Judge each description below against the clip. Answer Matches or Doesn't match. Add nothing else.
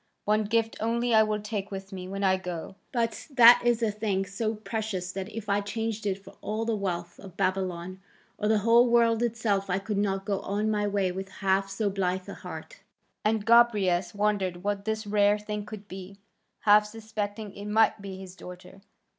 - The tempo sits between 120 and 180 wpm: Doesn't match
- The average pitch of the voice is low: Doesn't match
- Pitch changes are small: Matches